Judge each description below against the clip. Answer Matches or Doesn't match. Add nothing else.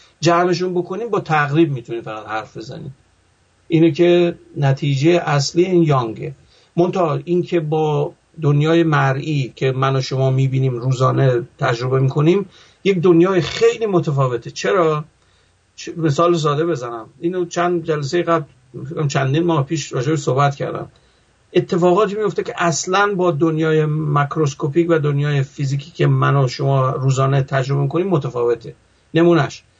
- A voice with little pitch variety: Doesn't match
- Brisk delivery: Doesn't match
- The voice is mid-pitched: Matches